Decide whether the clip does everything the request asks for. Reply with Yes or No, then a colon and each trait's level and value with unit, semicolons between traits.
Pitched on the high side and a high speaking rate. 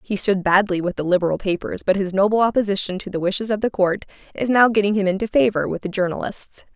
Yes: high, 200 Hz; fast, 230 wpm